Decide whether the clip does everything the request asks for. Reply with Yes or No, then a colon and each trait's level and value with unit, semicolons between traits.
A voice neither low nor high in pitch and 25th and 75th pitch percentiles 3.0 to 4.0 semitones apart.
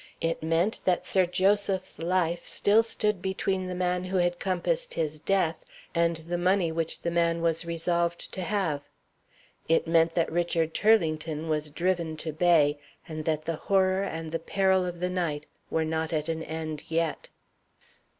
No: medium, 170 Hz; narrow, 2.4 semitones